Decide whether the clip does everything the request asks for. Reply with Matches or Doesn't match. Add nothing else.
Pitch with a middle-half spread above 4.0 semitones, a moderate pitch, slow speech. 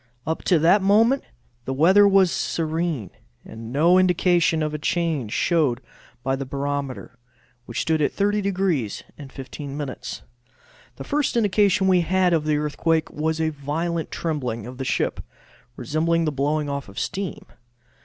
Doesn't match